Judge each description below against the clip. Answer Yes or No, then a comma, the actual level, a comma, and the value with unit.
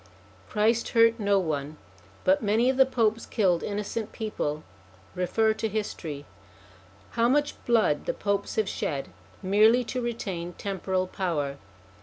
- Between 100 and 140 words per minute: Yes, slow, 135 wpm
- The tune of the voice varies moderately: Yes, average, 4.1 semitones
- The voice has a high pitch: Yes, high, 205 Hz